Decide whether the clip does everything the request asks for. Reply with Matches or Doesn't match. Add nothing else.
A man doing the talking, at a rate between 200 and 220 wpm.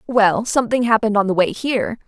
Doesn't match